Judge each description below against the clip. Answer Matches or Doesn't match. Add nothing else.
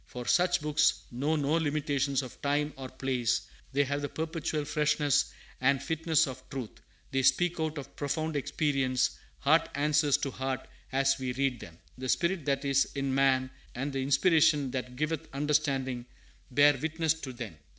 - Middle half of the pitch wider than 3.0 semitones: Doesn't match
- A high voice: Doesn't match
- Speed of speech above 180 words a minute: Doesn't match